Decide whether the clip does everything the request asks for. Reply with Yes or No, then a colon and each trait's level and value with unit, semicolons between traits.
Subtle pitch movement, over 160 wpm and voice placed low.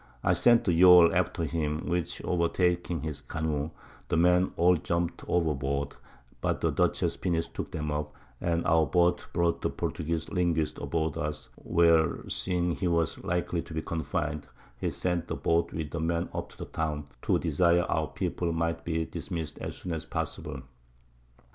Yes: narrow, 1.8 semitones; average, 175 wpm; very low, 85 Hz